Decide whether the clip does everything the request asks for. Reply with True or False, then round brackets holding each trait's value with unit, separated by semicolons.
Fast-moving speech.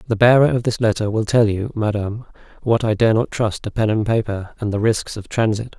True (240 wpm)